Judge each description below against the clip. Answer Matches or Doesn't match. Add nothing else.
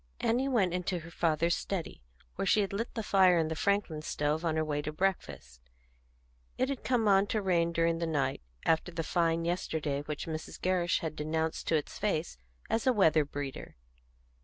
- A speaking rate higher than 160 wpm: Matches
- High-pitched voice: Doesn't match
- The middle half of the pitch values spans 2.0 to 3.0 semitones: Doesn't match